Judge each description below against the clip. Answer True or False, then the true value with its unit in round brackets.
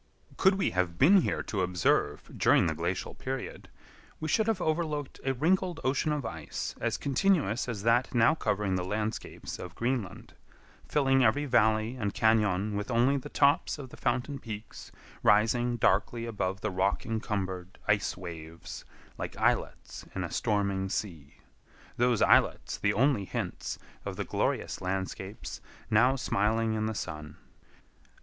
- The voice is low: True (110 Hz)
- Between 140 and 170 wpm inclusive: True (150 wpm)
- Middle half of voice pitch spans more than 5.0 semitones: True (5.6 semitones)